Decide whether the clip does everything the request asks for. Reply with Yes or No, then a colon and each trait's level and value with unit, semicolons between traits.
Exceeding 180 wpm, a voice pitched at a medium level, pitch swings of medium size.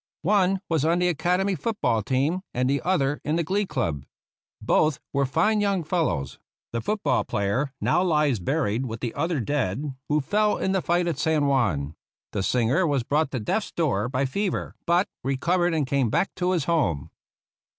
No: average, 190 wpm; medium, 150 Hz; wide, 5.8 semitones